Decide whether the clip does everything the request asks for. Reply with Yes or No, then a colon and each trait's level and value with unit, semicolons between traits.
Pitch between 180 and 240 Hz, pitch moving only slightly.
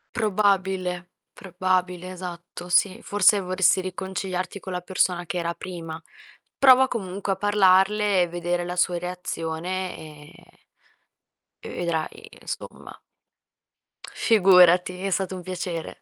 Yes: medium, 185 Hz; narrow, 1.4 semitones